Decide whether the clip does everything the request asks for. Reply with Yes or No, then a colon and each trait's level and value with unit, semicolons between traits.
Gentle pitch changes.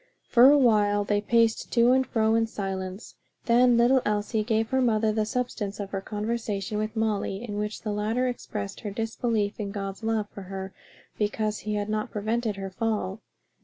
Yes: narrow, 2.0 semitones